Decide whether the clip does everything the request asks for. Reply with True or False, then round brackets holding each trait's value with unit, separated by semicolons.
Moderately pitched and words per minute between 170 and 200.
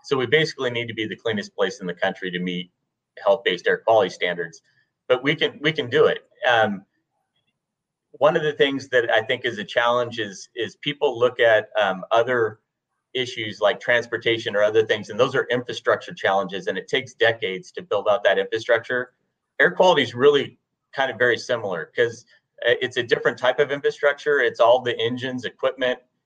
True (145 Hz; 190 wpm)